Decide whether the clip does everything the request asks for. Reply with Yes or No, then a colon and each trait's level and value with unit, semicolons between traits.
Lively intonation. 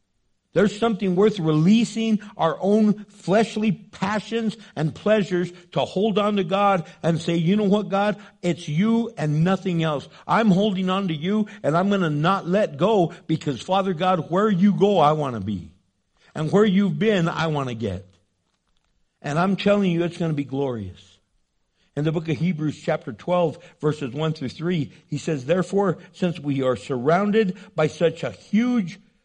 No: average, 5.0 semitones